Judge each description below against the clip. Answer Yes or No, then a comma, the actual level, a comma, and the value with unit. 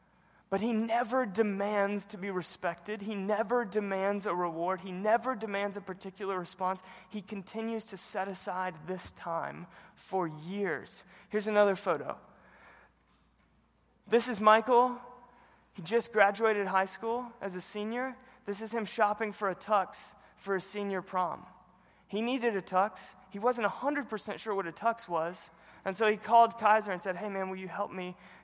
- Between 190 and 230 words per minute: No, average, 160 wpm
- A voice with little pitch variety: No, average, 3.0 semitones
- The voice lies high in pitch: Yes, high, 200 Hz